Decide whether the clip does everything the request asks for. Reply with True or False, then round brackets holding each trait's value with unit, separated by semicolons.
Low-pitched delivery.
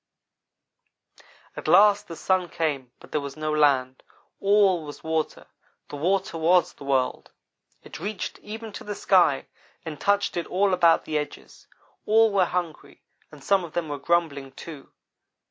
False (165 Hz)